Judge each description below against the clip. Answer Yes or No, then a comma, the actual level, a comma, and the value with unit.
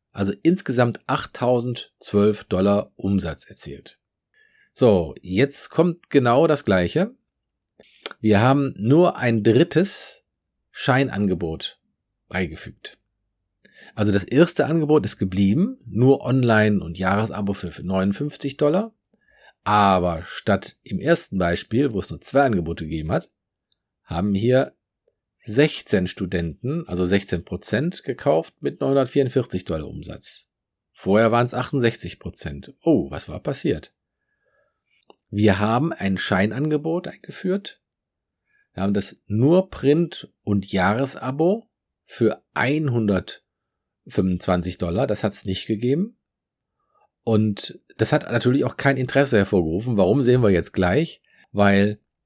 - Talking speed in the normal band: No, slow, 115 wpm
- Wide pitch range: Yes, wide, 6.3 semitones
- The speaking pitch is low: Yes, low, 115 Hz